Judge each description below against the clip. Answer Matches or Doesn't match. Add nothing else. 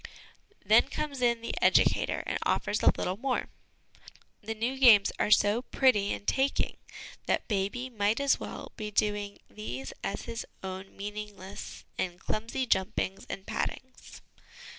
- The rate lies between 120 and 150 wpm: Matches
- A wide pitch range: Doesn't match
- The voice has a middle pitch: Doesn't match